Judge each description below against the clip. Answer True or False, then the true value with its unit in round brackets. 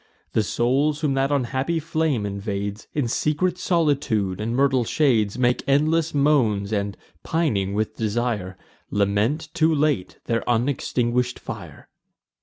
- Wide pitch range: True (5.9 semitones)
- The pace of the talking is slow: True (125 wpm)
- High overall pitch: False (125 Hz)